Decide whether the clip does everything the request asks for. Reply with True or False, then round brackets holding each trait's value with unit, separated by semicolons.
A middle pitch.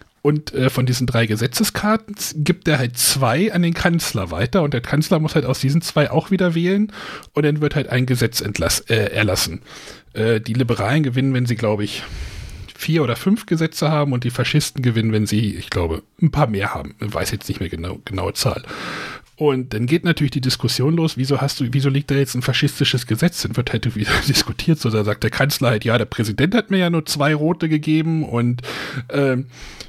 False (130 Hz)